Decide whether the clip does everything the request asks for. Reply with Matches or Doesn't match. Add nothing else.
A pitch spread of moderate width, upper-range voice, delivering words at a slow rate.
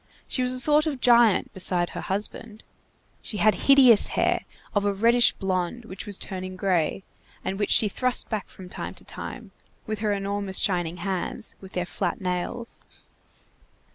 Doesn't match